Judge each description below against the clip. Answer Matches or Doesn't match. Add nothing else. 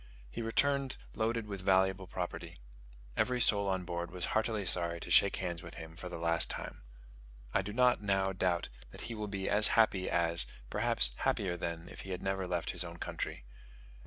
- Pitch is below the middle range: Matches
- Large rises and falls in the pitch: Doesn't match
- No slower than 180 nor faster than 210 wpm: Matches